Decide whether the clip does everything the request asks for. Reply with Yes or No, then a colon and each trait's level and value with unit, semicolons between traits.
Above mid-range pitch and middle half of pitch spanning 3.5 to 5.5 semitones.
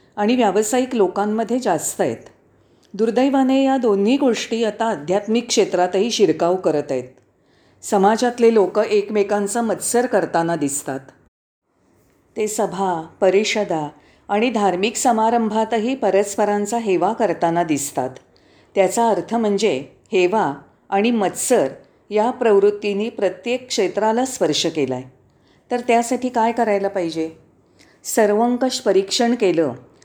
Yes: high, 205 Hz; average, 4.3 semitones